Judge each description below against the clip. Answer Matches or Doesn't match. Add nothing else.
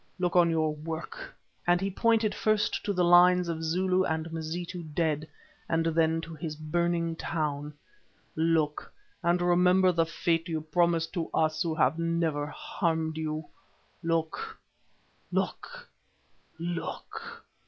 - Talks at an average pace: Doesn't match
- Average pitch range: Doesn't match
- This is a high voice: Doesn't match